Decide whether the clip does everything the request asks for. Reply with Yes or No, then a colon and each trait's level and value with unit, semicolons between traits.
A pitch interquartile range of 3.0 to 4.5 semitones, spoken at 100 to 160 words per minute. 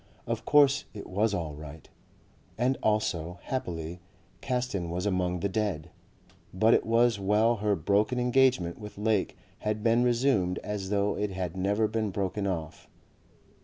Yes: average, 3.8 semitones; average, 150 wpm